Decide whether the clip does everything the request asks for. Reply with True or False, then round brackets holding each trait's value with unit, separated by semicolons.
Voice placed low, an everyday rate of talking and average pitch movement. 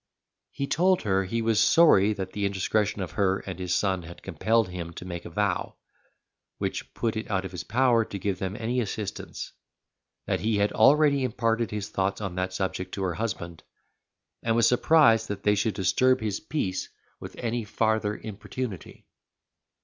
True (105 Hz; 180 wpm; 3.3 semitones)